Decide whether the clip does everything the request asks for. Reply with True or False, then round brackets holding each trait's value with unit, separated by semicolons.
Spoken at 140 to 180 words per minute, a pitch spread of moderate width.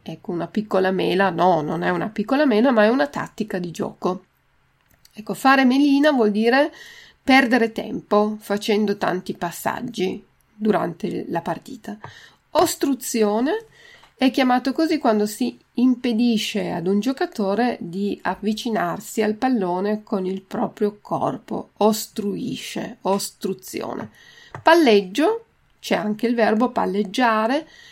False (120 wpm; 4.6 semitones)